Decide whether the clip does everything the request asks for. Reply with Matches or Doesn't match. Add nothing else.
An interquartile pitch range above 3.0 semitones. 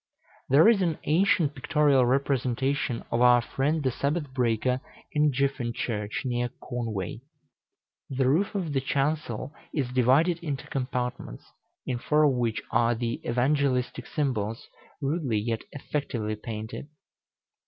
Matches